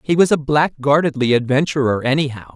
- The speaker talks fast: No, average, 140 wpm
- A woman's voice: No, male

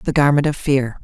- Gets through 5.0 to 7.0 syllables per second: Yes, 5.6 syllables/s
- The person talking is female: Yes, female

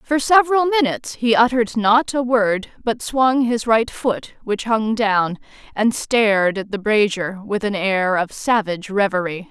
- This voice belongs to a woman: Yes, female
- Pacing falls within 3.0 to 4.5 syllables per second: Yes, 4.4 syllables/s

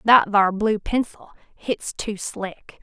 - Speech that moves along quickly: No, average, 150 wpm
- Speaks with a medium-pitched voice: No, high, 210 Hz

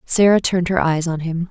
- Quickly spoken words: Yes, fast, 240 wpm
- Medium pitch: Yes, medium, 170 Hz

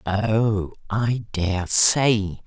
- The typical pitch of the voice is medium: No, low, 115 Hz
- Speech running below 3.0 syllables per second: Yes, 2.0 syllables/s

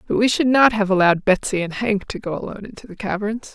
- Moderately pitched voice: No, high, 205 Hz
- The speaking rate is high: Yes, fast, 255 wpm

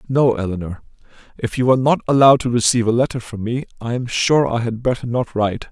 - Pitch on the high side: No, low, 120 Hz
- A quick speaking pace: Yes, fast, 220 wpm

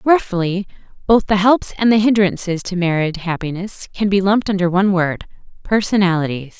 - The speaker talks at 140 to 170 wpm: Yes, average, 145 wpm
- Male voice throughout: No, female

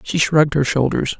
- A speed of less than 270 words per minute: Yes, average, 200 wpm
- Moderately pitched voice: Yes, medium, 145 Hz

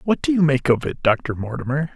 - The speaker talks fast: Yes, fast, 245 wpm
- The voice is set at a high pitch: No, medium, 145 Hz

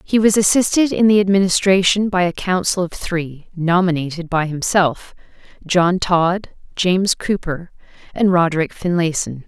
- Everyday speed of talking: No, slow, 125 wpm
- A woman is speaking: Yes, female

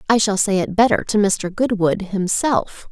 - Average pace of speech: Yes, average, 185 wpm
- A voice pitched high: Yes, high, 205 Hz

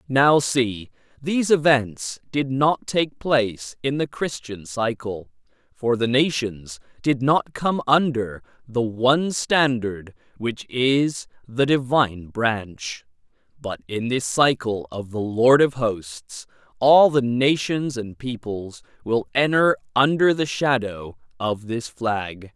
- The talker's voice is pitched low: Yes, low, 125 Hz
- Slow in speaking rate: Yes, slow, 130 wpm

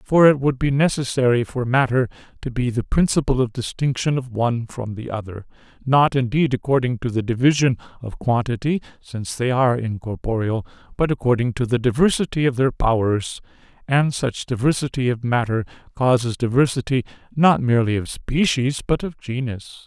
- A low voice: Yes, low, 125 Hz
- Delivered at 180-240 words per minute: No, average, 155 wpm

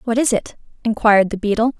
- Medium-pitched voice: No, high, 220 Hz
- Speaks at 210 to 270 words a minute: No, average, 200 wpm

